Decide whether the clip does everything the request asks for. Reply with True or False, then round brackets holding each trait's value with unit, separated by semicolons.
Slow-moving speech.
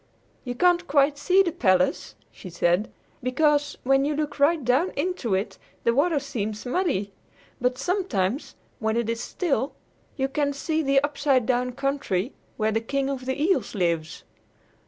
False (160 wpm)